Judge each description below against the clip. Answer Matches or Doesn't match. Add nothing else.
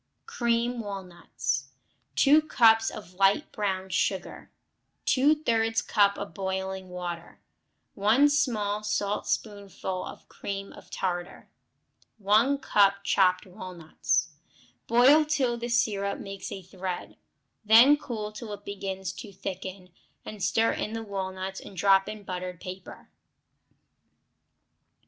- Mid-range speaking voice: Doesn't match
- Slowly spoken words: Matches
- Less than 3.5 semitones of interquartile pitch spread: Matches